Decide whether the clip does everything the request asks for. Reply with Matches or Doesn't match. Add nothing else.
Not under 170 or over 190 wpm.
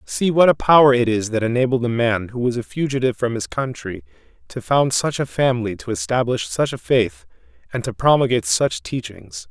Doesn't match